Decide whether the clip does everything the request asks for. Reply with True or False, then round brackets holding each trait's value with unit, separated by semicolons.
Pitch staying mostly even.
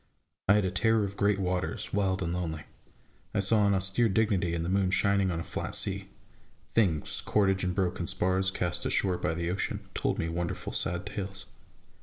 True (2.0 semitones)